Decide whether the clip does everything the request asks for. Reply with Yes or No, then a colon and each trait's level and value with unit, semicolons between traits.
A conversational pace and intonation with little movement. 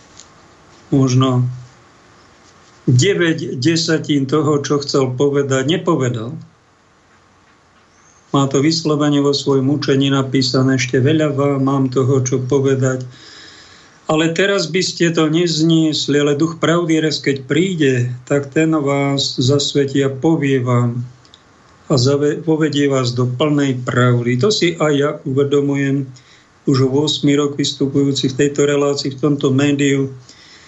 Yes: average, 120 wpm; narrow, 2.2 semitones